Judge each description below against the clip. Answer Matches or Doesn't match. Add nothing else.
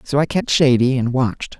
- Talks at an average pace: Doesn't match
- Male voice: Matches